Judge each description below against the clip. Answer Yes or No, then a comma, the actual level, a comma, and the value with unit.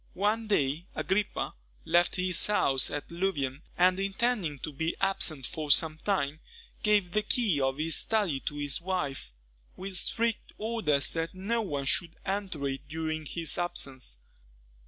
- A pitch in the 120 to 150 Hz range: No, medium, 170 Hz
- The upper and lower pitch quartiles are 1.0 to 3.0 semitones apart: No, average, 5.2 semitones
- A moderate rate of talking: Yes, average, 150 wpm